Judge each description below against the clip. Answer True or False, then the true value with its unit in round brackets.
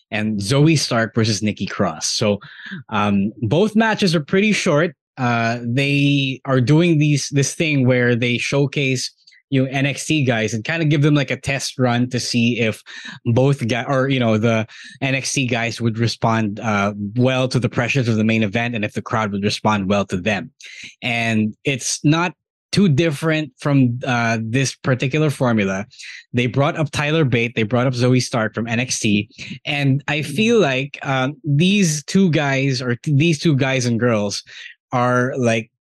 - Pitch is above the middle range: False (130 Hz)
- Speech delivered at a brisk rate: False (180 wpm)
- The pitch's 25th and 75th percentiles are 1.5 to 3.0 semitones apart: False (3.9 semitones)